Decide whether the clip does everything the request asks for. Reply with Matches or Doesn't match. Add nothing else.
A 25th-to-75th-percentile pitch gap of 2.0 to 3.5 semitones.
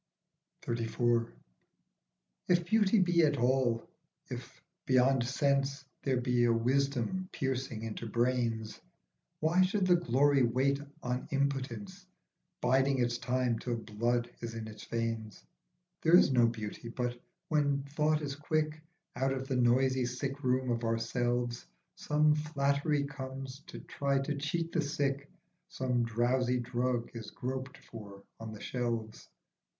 Matches